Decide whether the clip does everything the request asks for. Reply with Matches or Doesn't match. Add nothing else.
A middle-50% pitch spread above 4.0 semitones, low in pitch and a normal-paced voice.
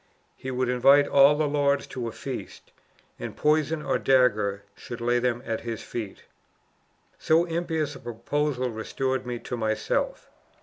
Doesn't match